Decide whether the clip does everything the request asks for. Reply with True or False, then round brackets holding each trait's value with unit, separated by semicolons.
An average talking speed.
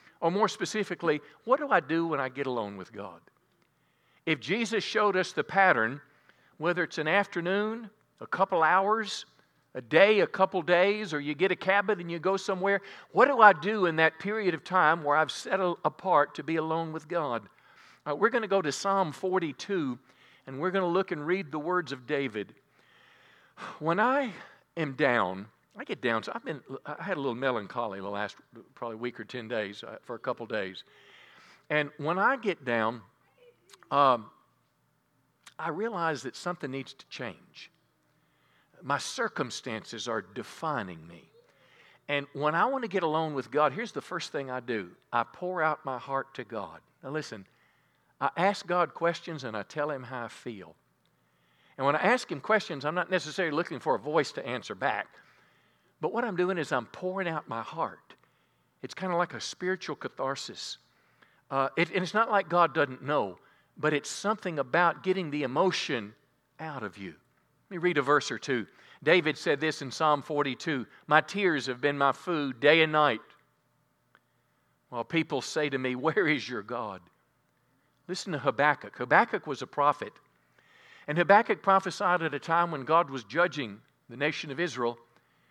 True (185 wpm)